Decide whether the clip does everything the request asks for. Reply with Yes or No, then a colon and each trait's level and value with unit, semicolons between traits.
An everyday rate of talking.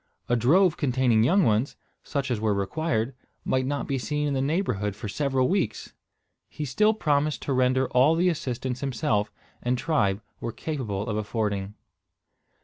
Yes: average, 160 wpm